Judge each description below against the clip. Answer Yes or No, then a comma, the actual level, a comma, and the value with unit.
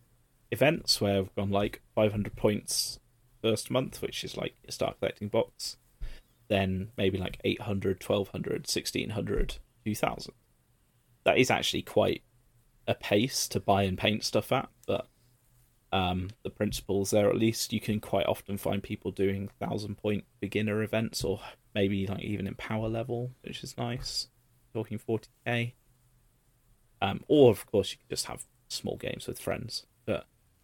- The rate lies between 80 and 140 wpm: No, average, 155 wpm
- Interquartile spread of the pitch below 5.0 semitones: Yes, average, 3.3 semitones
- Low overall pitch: Yes, low, 110 Hz